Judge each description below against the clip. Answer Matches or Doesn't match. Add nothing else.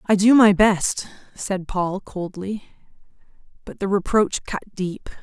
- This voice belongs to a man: Doesn't match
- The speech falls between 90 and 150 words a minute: Matches